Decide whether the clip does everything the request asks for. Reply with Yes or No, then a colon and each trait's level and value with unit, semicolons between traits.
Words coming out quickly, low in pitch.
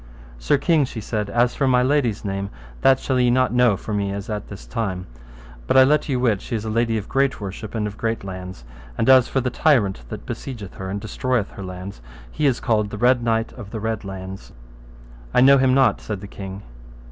Yes: fast, 230 wpm; low, 115 Hz